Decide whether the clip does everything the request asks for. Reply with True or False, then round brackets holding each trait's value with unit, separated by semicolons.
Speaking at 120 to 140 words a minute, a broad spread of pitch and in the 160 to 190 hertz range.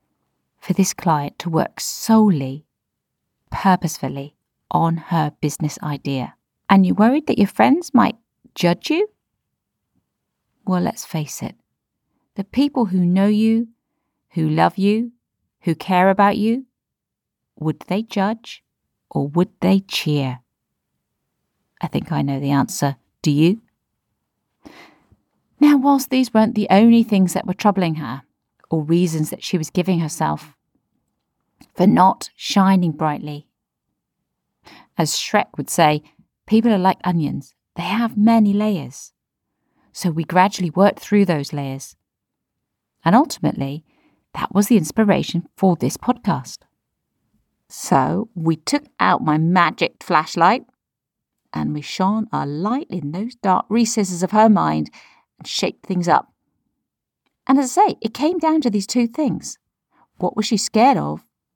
True (135 wpm; 6.0 semitones; 185 Hz)